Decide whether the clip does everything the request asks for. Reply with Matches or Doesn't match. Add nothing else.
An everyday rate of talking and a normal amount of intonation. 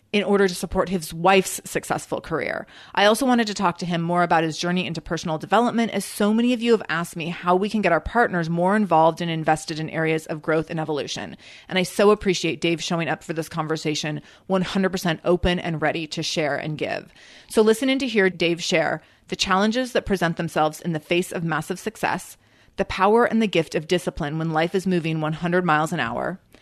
Doesn't match